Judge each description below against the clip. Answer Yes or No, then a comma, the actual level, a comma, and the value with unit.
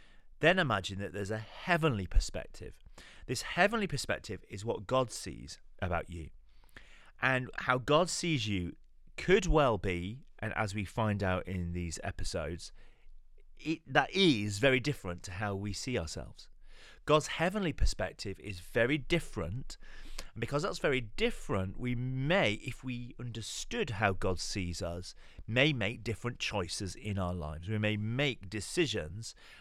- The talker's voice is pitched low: Yes, low, 110 Hz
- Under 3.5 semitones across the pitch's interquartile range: No, wide, 5.6 semitones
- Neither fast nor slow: Yes, average, 150 wpm